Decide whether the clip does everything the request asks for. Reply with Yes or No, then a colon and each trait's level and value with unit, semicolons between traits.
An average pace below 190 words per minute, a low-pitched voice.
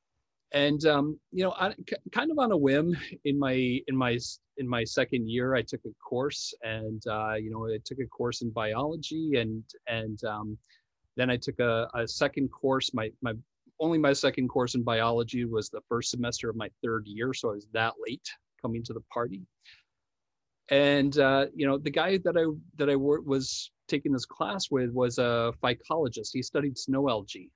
No: average, 195 wpm; low, 125 Hz